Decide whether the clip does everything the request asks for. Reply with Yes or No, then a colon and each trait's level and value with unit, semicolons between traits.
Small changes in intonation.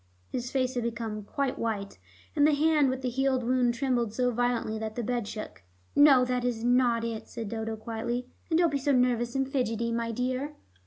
Yes: narrow, 2.2 semitones